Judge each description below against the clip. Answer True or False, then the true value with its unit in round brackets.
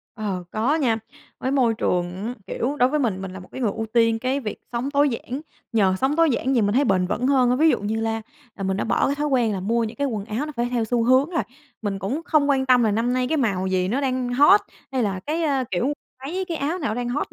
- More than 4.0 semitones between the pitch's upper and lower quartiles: True (4.6 semitones)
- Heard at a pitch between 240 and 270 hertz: True (245 Hz)